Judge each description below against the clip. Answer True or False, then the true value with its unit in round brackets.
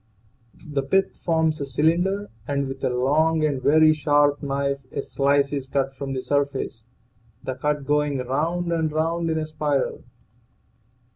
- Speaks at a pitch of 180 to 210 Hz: False (145 Hz)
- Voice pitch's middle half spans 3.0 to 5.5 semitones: False (2.4 semitones)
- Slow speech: False (155 wpm)